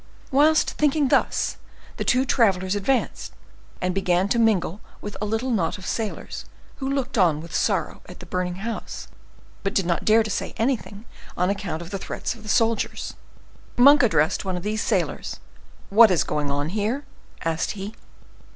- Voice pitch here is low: No, high, 205 Hz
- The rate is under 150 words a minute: No, average, 170 wpm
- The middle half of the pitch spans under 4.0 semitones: No, average, 4.3 semitones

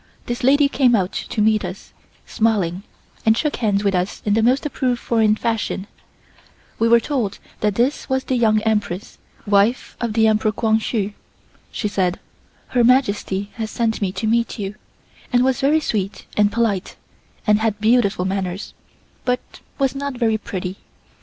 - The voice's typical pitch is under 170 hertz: No, high, 220 Hz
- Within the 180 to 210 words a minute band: No, average, 170 wpm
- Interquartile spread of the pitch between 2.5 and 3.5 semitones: Yes, average, 3.2 semitones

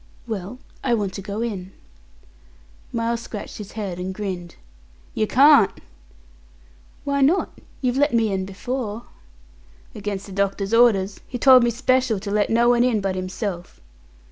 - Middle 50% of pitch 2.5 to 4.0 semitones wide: Yes, average, 3.7 semitones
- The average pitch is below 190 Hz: No, high, 215 Hz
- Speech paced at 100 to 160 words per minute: Yes, average, 150 wpm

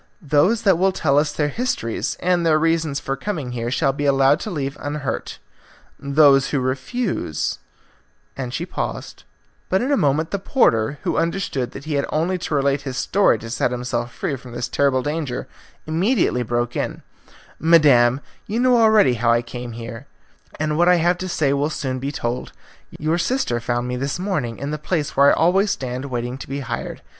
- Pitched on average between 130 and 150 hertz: Yes, medium, 140 Hz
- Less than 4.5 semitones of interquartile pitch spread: No, average, 5.3 semitones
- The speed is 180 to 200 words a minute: Yes, average, 195 wpm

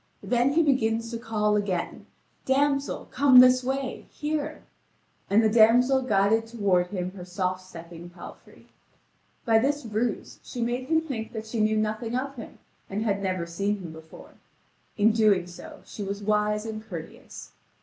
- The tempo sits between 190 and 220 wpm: No, average, 160 wpm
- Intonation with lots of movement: No, average, 4.1 semitones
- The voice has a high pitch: Yes, high, 220 Hz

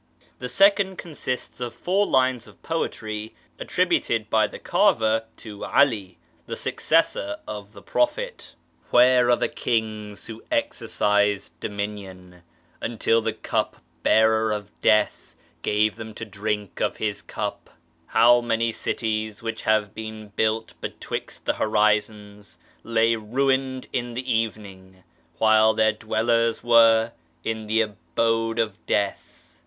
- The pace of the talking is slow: Yes, slow, 130 wpm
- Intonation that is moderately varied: No, narrow, 1.9 semitones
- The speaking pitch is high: No, low, 110 Hz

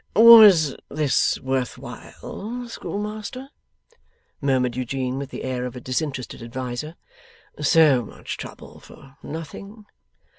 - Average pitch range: No, wide, 7.8 semitones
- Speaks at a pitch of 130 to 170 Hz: Yes, medium, 140 Hz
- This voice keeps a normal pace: No, slow, 110 wpm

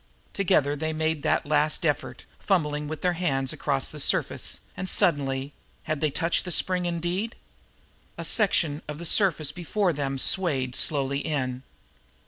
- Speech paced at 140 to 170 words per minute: Yes, average, 155 wpm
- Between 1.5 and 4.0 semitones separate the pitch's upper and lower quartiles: Yes, average, 3.5 semitones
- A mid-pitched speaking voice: Yes, medium, 155 Hz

